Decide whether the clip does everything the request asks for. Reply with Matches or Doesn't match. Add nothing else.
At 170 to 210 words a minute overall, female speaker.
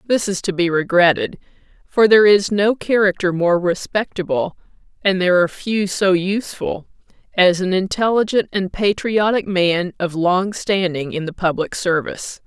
Doesn't match